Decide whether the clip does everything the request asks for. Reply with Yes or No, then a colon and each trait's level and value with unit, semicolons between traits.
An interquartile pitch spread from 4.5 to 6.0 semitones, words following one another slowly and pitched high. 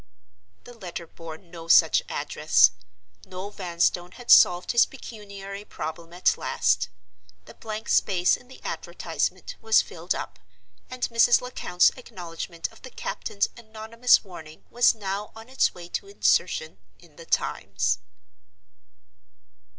Yes: average, 5.1 semitones; slow, 130 wpm; high, 195 Hz